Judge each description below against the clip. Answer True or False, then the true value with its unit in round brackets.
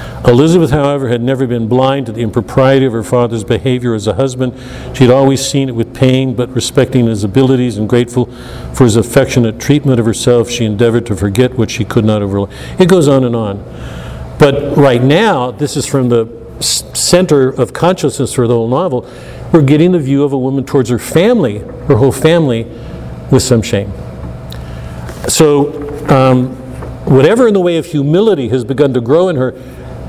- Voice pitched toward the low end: True (125 Hz)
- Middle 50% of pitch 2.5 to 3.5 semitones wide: True (3.2 semitones)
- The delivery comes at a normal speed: True (185 wpm)